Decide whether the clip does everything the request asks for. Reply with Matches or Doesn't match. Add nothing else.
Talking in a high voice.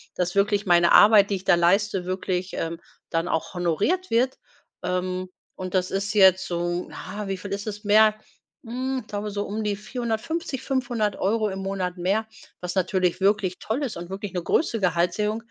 Matches